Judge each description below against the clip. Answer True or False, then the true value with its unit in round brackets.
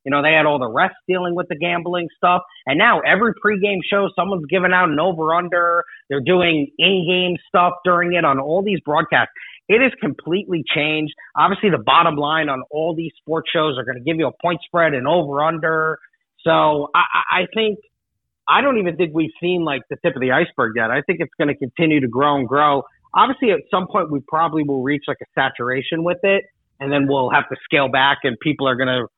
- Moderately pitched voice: True (165 Hz)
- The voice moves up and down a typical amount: True (3.7 semitones)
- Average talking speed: False (225 wpm)